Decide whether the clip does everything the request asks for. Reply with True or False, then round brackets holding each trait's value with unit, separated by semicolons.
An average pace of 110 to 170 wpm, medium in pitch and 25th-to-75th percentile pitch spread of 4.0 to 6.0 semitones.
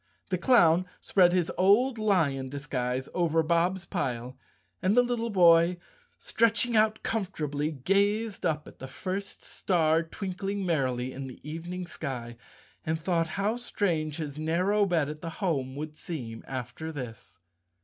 True (150 wpm; 165 Hz; 5.3 semitones)